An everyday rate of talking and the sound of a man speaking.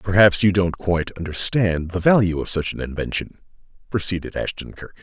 Yes: average, 165 wpm; male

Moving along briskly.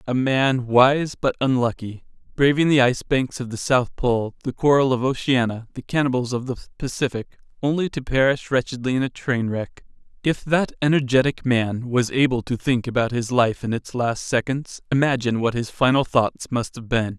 No: average, 185 wpm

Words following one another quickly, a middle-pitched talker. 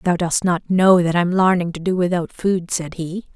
Yes: fast, 230 wpm; medium, 175 Hz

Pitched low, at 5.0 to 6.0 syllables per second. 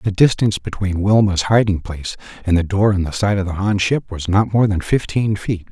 Yes: low, 100 Hz; 5.4 syllables/s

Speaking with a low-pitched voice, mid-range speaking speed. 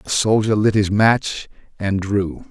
Yes: low, 105 Hz; average, 170 wpm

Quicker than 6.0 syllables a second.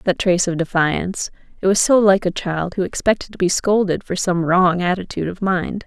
No: 5.4 syllables/s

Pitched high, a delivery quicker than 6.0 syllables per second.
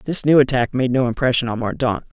No: low, 130 Hz; 6.2 syllables/s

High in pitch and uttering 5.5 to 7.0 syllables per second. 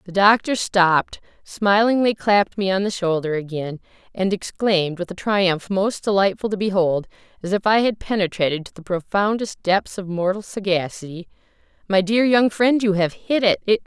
No: high, 195 Hz; 5.0 syllables/s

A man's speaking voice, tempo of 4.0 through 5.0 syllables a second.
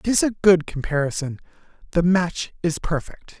Yes: male; 4.8 syllables/s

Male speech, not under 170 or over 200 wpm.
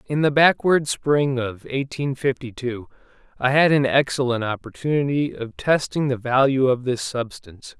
No: male; average, 155 wpm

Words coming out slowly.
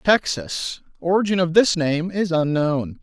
Yes: slow, 120 wpm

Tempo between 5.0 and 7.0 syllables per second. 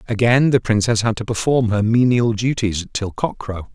No: 4.8 syllables/s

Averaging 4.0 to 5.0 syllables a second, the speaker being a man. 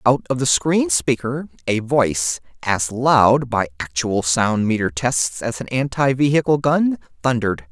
Yes: 4.2 syllables/s; male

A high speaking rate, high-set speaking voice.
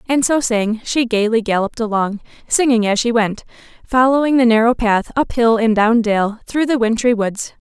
No: average, 190 wpm; high, 230 Hz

